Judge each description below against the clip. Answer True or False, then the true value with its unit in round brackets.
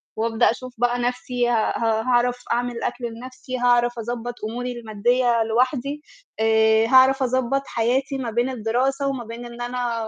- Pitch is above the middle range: True (245 Hz)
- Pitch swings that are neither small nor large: False (1.7 semitones)